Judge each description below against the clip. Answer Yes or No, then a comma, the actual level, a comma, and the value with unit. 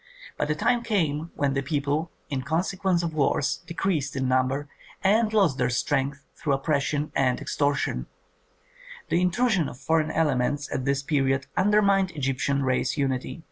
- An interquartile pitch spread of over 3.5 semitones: Yes, average, 4.0 semitones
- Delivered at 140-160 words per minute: Yes, average, 150 wpm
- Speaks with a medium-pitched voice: Yes, medium, 145 Hz